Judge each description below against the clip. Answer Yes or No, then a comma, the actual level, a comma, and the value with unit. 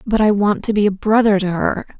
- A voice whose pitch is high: Yes, high, 205 Hz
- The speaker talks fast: Yes, fast, 270 wpm